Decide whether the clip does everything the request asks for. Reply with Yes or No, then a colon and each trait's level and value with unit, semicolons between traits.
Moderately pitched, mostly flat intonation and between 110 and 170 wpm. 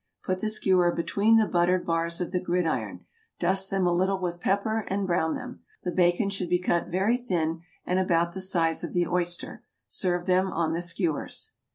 No: medium, 180 Hz; narrow, 1.9 semitones; average, 195 wpm